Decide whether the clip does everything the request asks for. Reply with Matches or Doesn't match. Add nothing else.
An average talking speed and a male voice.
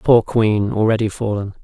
Matches